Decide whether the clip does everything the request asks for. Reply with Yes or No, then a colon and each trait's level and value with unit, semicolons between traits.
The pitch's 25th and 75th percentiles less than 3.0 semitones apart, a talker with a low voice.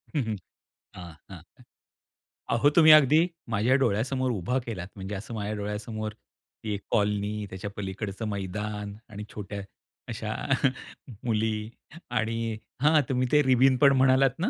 No: average, 3.7 semitones; low, 110 Hz